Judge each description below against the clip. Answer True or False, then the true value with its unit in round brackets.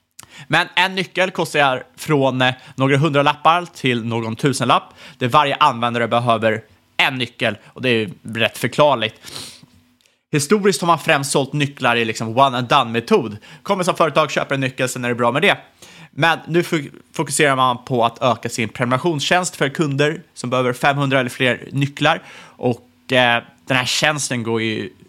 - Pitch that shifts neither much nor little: True (4.6 semitones)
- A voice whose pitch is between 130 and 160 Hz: True (135 Hz)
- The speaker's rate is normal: True (170 wpm)